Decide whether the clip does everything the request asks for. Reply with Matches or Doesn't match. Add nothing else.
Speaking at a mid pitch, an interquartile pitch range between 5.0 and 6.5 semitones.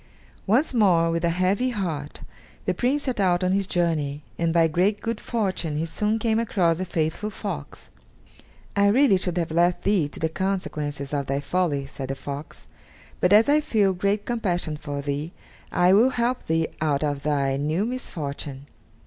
Matches